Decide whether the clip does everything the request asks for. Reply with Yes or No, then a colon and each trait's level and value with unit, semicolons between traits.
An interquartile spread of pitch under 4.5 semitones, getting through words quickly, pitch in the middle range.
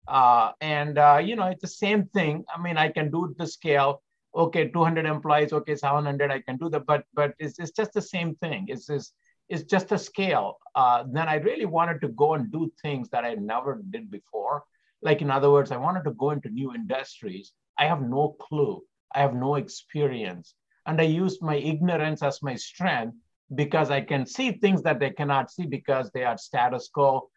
Yes: average, 3.9 semitones; fast, 210 wpm; medium, 155 Hz